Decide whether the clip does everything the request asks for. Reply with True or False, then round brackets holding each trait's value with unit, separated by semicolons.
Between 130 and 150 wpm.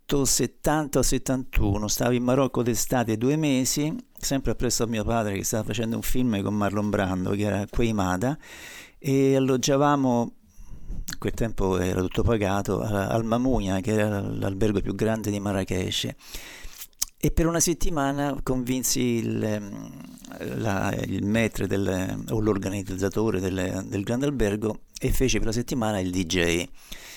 True (135 wpm)